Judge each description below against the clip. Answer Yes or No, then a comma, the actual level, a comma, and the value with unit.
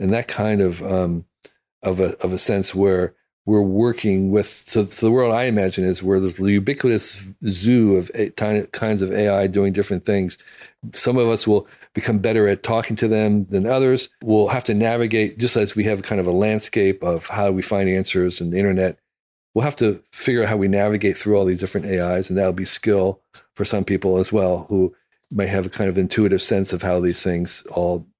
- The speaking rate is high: Yes, fast, 215 wpm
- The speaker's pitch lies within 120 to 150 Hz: No, low, 100 Hz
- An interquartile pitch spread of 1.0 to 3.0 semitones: Yes, narrow, 2.4 semitones